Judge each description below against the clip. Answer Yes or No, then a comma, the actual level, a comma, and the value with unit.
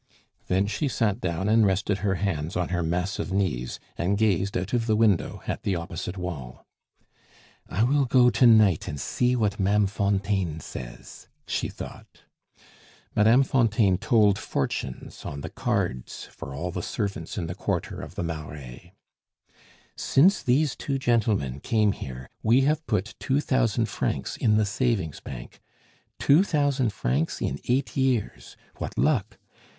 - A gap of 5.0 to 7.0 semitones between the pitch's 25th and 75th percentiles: Yes, wide, 5.4 semitones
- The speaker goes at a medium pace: Yes, average, 155 wpm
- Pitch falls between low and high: No, low, 100 Hz